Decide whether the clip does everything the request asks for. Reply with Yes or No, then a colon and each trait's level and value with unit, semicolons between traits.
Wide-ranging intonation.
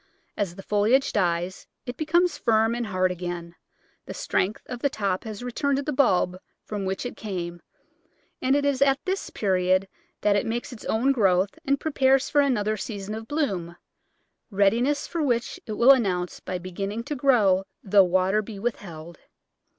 Yes: wide, 5.8 semitones